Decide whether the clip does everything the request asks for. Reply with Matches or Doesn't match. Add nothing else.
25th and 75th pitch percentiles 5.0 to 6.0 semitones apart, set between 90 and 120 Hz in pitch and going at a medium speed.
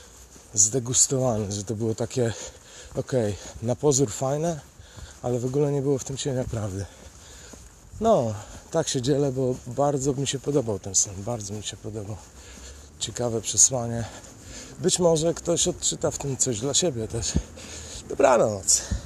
Matches